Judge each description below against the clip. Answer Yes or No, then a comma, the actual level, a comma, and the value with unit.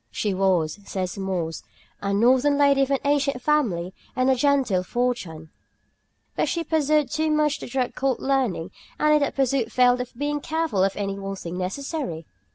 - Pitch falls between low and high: No, very high, 250 Hz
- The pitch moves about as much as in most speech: No, wide, 6.7 semitones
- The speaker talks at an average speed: Yes, average, 175 wpm